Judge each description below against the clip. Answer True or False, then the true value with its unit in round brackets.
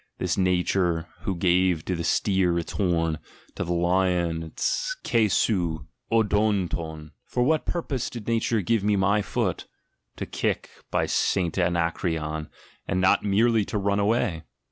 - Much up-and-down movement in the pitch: False (3.6 semitones)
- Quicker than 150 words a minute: False (140 wpm)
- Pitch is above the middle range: False (95 Hz)